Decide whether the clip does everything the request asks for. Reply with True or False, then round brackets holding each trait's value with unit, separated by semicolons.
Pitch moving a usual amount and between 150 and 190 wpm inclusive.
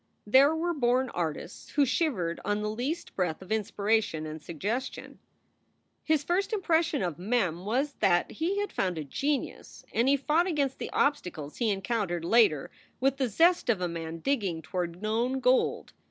False (7.9 semitones; 170 wpm)